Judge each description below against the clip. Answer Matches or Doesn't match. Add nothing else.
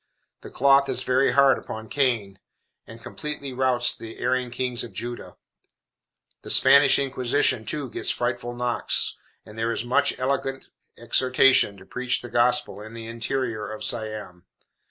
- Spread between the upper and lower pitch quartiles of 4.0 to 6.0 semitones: Doesn't match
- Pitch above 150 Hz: Doesn't match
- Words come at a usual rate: Matches